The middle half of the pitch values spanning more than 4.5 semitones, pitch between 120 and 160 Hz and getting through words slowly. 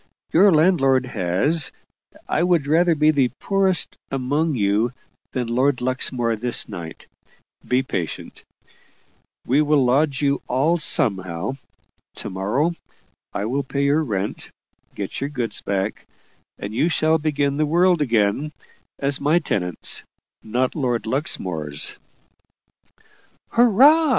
Yes: wide, 5.4 semitones; low, 135 Hz; slow, 120 wpm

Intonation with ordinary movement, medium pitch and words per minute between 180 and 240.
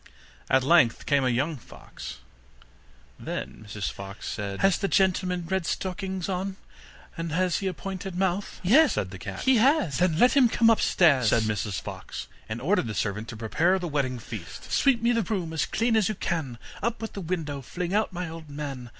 No: wide, 7.2 semitones; medium, 175 Hz; average, 200 wpm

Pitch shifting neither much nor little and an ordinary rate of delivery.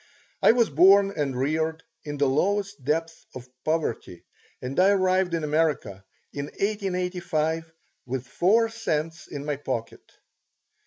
No: average, 4.7 semitones; slow, 130 wpm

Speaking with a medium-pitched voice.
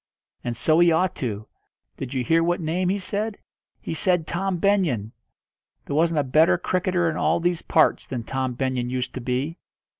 Yes: medium, 160 Hz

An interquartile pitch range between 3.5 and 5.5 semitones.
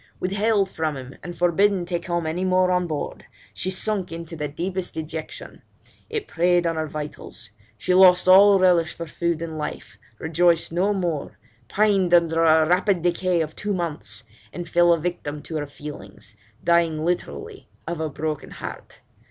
No: narrow, 2.6 semitones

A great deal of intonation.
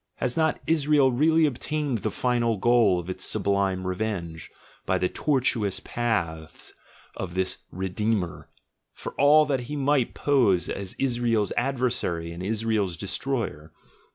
Yes: wide, 6.2 semitones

